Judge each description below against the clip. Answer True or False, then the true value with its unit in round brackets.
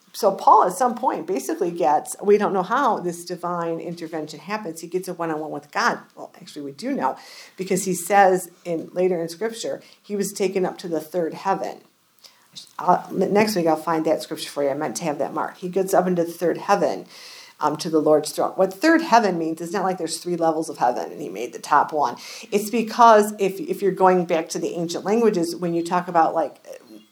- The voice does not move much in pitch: False (3.5 semitones)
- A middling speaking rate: False (220 wpm)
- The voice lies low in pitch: False (180 Hz)